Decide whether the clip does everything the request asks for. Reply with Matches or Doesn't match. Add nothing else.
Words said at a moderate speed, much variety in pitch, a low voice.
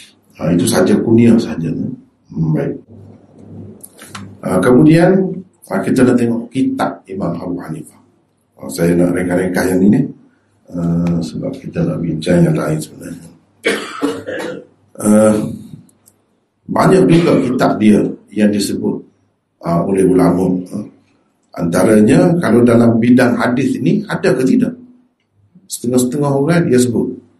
Matches